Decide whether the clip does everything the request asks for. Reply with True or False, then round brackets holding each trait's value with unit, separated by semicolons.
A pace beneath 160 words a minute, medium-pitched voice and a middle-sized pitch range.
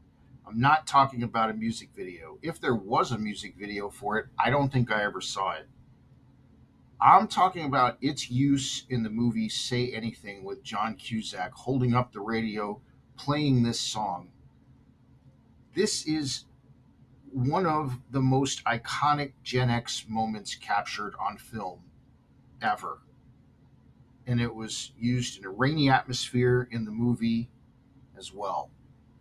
False (140 wpm; 125 Hz; 3.0 semitones)